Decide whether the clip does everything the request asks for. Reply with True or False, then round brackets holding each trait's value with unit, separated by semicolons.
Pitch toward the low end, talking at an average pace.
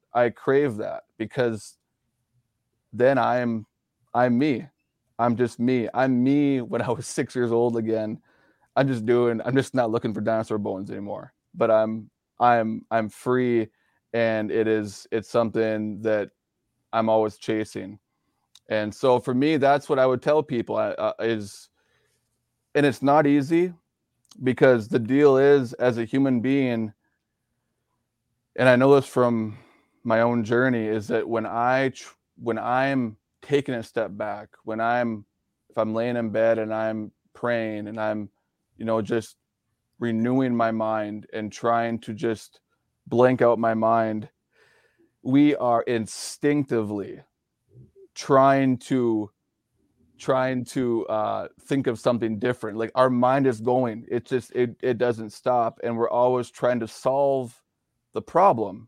True (120 Hz; 150 wpm)